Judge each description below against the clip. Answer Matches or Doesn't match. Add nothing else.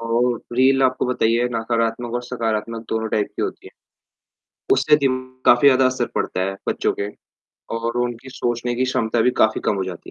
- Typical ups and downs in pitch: Doesn't match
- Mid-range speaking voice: Doesn't match